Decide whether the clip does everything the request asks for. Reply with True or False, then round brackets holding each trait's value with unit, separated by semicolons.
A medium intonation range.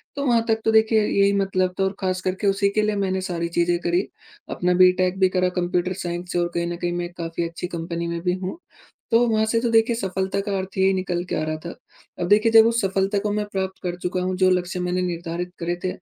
False (2.2 semitones)